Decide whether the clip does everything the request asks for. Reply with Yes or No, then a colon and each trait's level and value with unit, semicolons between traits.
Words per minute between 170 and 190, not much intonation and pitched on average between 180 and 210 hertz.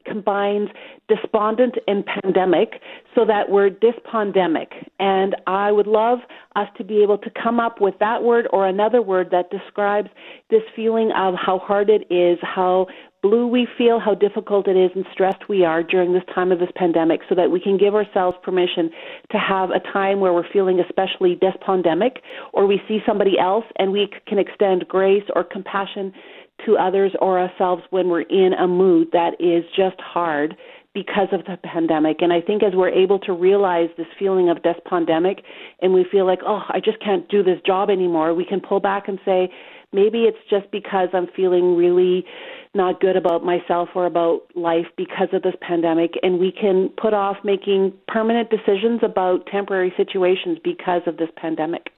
Yes: average, 185 wpm; narrow, 2.2 semitones; high, 190 Hz